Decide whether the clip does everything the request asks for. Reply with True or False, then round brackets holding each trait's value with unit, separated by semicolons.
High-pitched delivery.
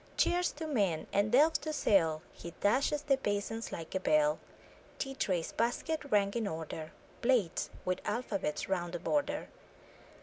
True (210 Hz)